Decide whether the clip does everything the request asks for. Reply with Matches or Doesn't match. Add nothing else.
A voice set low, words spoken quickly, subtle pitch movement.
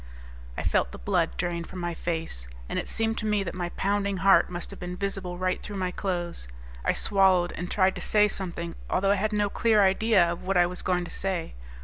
Doesn't match